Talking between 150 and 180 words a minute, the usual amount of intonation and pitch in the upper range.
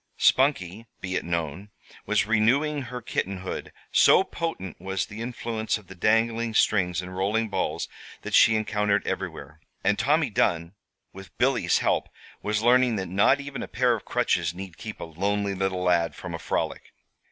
No: average, 165 wpm; average, 4.0 semitones; low, 105 Hz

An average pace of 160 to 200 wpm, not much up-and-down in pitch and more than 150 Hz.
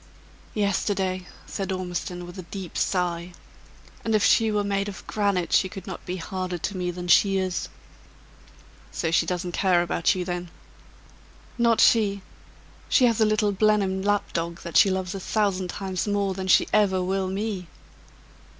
Yes: average, 165 wpm; narrow, 2.1 semitones; high, 190 Hz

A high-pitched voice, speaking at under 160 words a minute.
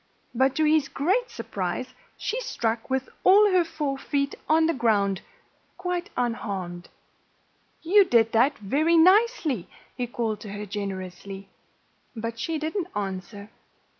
Yes: very high, 260 Hz; slow, 135 wpm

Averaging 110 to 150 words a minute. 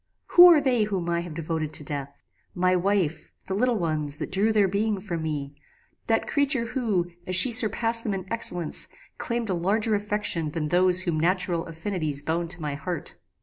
No: average, 190 wpm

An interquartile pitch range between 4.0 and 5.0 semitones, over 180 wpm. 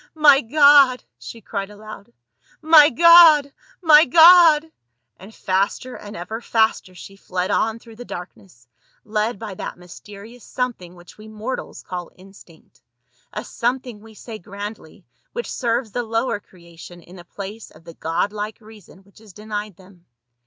No: average, 4.6 semitones; average, 165 wpm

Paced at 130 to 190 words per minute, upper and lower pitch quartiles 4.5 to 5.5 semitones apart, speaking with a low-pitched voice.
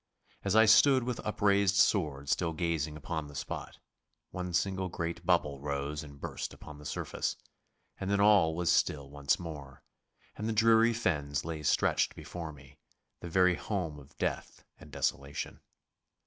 Yes: average, 160 wpm; average, 5.2 semitones; very low, 85 Hz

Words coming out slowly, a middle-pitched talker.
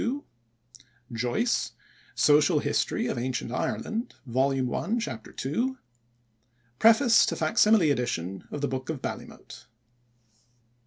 Yes: slow, 115 wpm; medium, 145 Hz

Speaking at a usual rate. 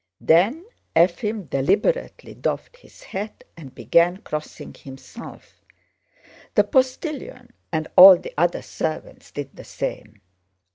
No: slow, 110 wpm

